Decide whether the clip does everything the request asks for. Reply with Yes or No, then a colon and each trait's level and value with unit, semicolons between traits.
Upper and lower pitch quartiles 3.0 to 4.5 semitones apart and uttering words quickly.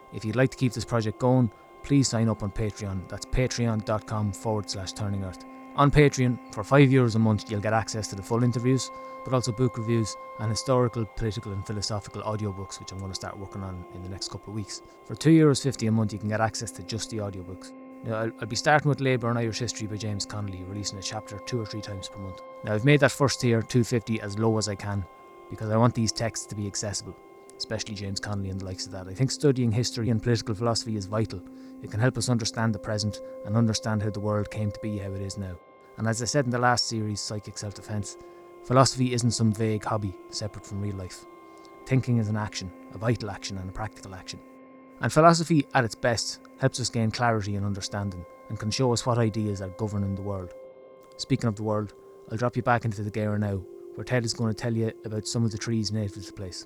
Yes: average, 3.4 semitones; fast, 240 wpm